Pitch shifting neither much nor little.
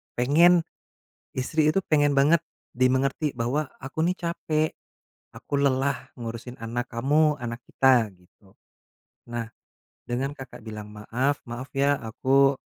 Yes: average, 3.5 semitones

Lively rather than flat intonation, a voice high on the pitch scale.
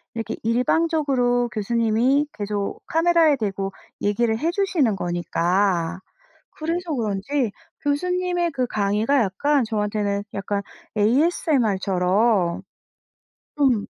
Yes: wide, 6.3 semitones; high, 230 Hz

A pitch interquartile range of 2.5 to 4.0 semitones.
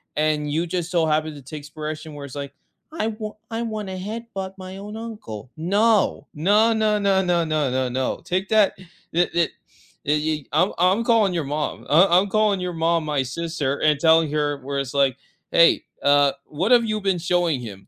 No: average, 5.2 semitones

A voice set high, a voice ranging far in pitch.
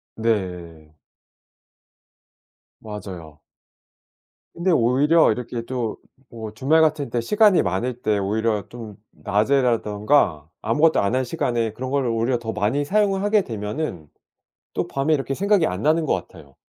No: low, 115 Hz; wide, 5.9 semitones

